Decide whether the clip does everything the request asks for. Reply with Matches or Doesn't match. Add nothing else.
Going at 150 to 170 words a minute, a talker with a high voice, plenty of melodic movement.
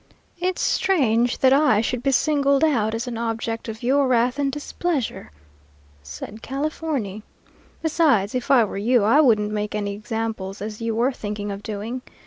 Doesn't match